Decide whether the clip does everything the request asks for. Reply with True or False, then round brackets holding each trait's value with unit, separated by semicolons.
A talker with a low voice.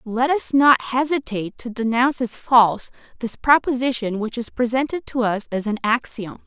False (240 Hz)